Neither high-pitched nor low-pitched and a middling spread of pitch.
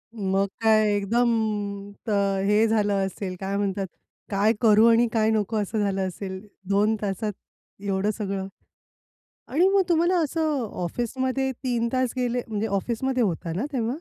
No: high, 215 Hz; average, 3.5 semitones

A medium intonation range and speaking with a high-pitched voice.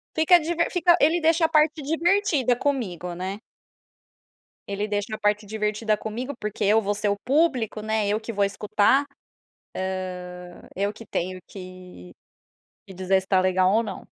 No: wide, 6.4 semitones; high, 215 Hz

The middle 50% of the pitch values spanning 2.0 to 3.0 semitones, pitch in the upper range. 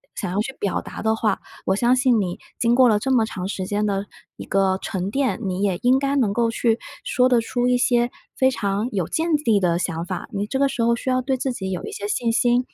No: average, 4.2 semitones; high, 225 Hz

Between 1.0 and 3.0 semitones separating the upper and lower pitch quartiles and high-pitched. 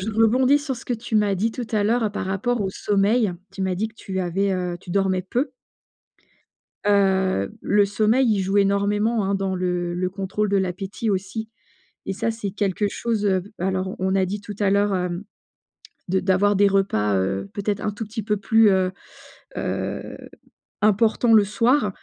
Yes: narrow, 2.4 semitones; high, 200 Hz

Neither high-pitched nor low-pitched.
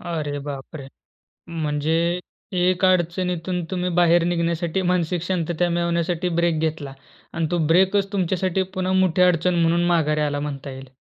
Yes: medium, 170 Hz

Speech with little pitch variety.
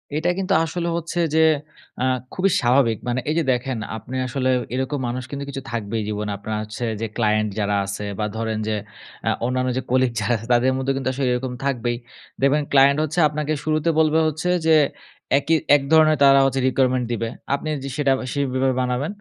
No: average, 3.3 semitones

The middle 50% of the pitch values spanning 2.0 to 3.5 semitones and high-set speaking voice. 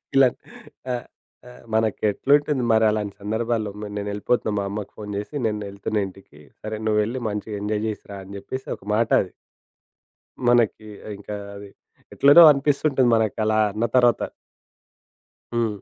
No: average, 2.7 semitones; low, 110 Hz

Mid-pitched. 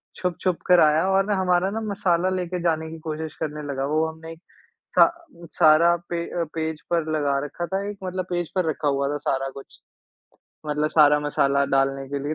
Yes: medium, 160 Hz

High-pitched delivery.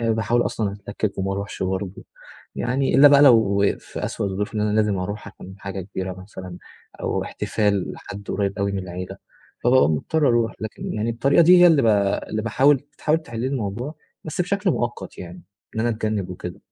No: low, 105 Hz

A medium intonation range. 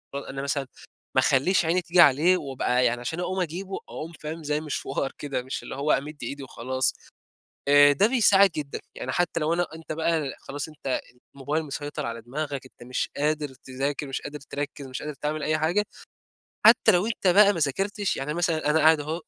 Yes: average, 3.4 semitones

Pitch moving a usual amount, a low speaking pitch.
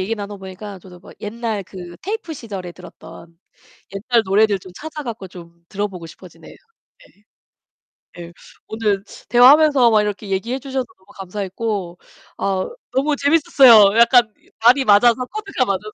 No: average, 4.5 semitones; high, 210 Hz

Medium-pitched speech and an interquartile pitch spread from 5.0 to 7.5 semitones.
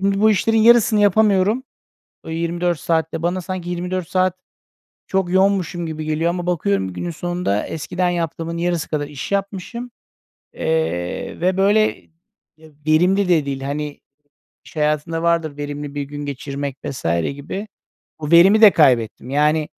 No: medium, 170 Hz; average, 4.1 semitones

